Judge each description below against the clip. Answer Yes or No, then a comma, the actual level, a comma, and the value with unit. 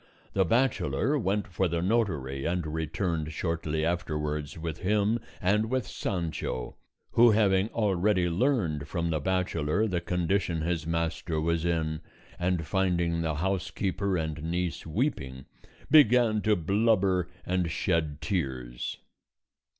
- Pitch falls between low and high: No, very low, 85 Hz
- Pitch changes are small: No, average, 3.9 semitones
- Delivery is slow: Yes, slow, 125 wpm